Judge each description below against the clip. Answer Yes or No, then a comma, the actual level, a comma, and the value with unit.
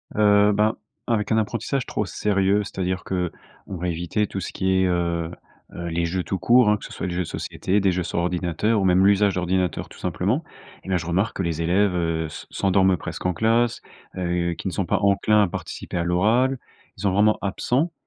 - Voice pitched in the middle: No, very low, 95 Hz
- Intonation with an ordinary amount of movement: Yes, average, 3.0 semitones